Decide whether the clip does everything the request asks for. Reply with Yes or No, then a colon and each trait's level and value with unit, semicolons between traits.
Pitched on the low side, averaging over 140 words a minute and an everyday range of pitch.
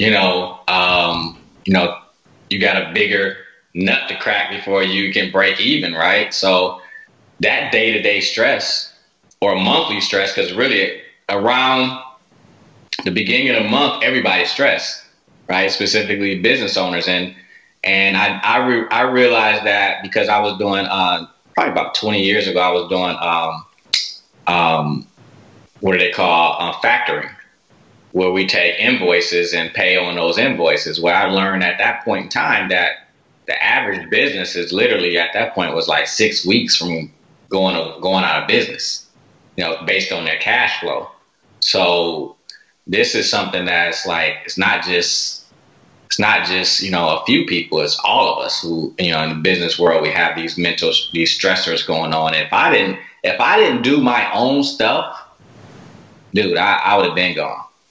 No: very low, 95 Hz; average, 170 wpm; wide, 6.8 semitones